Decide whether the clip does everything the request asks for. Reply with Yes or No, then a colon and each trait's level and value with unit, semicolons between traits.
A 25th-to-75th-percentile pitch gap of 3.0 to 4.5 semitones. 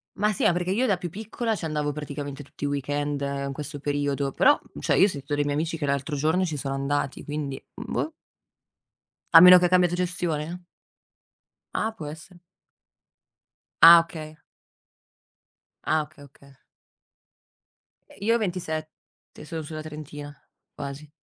Yes: average, 3.6 semitones